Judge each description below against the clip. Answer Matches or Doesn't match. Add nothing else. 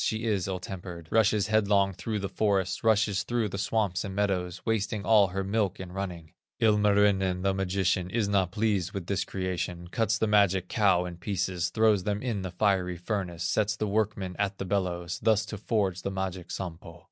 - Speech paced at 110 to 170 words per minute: Doesn't match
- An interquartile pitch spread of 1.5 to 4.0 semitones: Matches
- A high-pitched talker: Doesn't match